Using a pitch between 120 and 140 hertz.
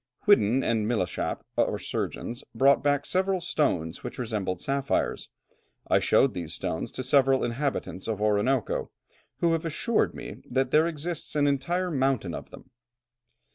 Yes: low, 135 Hz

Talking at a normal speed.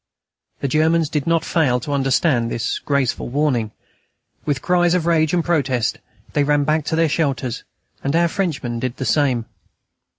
Yes: average, 165 wpm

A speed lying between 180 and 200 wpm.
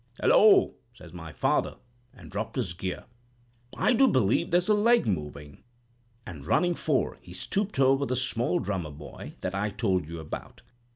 No: average, 165 wpm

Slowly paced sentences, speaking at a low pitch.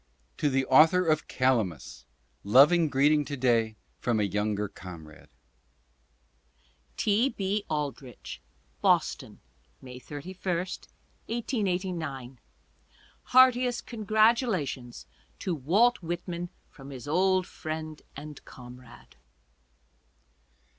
No: slow, 90 wpm; medium, 150 Hz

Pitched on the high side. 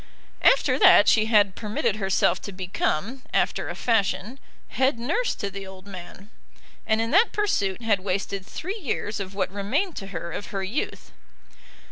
Yes: high, 205 Hz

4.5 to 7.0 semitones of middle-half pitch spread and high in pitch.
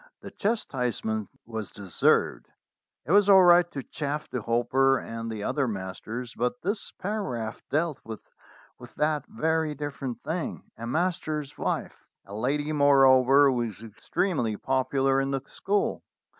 No: average, 4.9 semitones; low, 135 Hz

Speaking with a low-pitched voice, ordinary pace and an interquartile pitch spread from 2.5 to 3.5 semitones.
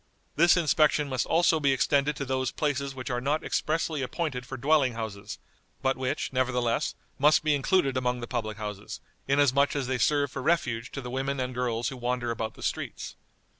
Yes: low, 130 Hz; average, 190 wpm; average, 2.8 semitones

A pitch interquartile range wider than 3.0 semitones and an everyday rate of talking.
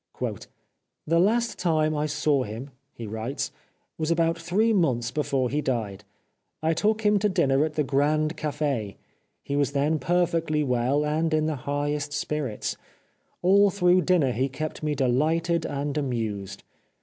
Yes: average, 3.7 semitones; average, 160 wpm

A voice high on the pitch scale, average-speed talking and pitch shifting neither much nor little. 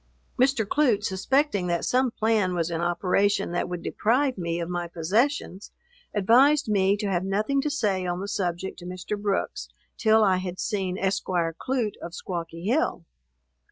Yes: high, 195 Hz; average, 165 wpm; average, 4.0 semitones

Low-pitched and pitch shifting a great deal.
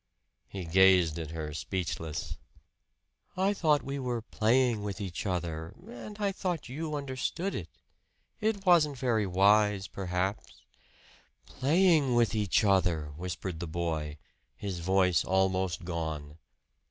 Yes: very low, 95 Hz; wide, 7.5 semitones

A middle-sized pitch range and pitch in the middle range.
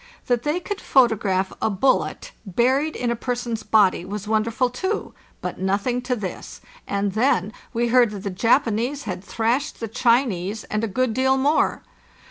No: average, 3.8 semitones; high, 230 Hz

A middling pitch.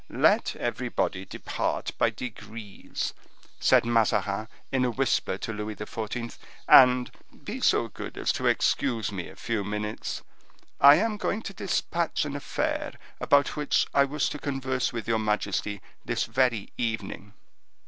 No: low, 115 Hz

